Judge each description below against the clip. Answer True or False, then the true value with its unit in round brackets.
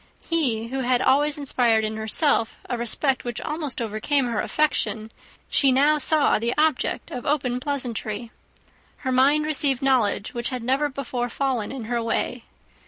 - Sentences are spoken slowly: False (160 wpm)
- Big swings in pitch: False (3.4 semitones)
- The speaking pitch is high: True (255 Hz)